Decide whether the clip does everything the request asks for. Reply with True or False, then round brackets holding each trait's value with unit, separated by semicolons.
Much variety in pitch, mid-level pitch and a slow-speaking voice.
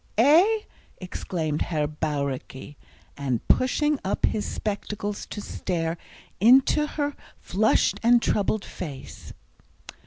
False (8.5 semitones; 200 Hz; 100 wpm)